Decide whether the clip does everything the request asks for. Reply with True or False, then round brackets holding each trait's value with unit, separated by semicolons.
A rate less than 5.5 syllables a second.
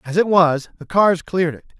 False (5.6 syllables/s)